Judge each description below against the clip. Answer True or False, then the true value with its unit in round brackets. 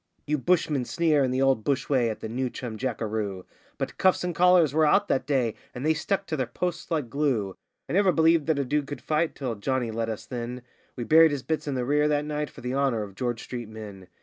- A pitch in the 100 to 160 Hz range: True (135 Hz)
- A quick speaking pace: True (245 wpm)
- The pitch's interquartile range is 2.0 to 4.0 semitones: False (4.7 semitones)